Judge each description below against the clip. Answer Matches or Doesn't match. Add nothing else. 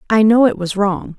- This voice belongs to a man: Doesn't match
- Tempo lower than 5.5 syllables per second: Matches